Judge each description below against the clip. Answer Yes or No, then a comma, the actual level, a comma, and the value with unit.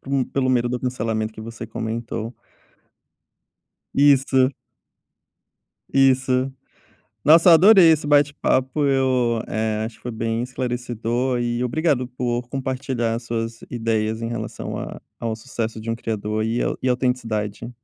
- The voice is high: No, low, 120 Hz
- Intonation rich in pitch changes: No, narrow, 2.5 semitones